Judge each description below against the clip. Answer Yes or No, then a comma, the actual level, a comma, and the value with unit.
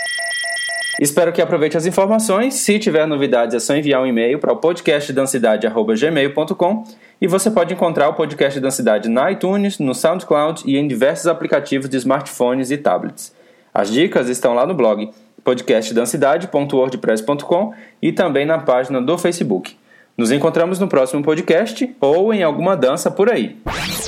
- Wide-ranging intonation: Yes, wide, 6.0 semitones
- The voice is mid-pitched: Yes, medium, 160 Hz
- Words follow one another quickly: No, average, 145 wpm